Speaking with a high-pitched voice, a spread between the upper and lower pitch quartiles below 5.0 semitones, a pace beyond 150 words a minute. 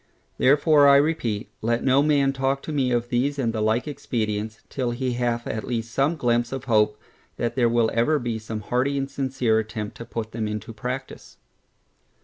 No: low, 120 Hz; average, 3.4 semitones; average, 190 wpm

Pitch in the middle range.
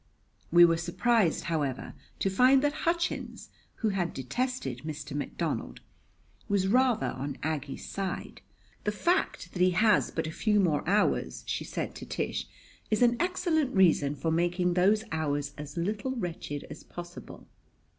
Yes: medium, 180 Hz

